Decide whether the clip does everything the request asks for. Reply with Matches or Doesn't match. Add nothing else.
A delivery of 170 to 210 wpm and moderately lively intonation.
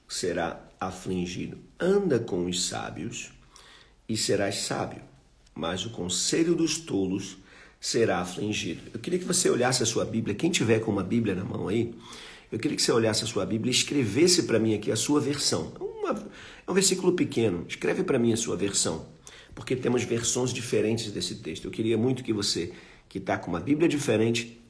Matches